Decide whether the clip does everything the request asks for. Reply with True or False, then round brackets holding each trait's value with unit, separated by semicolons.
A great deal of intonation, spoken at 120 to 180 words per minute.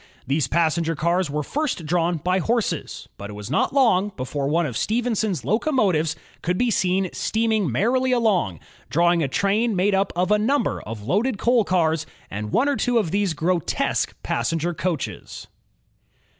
True (5.8 semitones; 170 wpm)